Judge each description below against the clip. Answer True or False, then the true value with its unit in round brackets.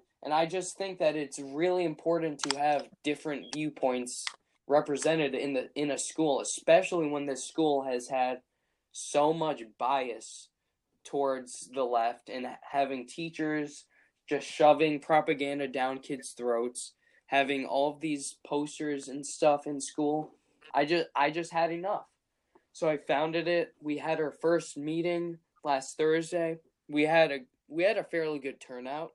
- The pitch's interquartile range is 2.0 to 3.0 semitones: True (2.5 semitones)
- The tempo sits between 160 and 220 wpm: False (150 wpm)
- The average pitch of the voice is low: False (150 Hz)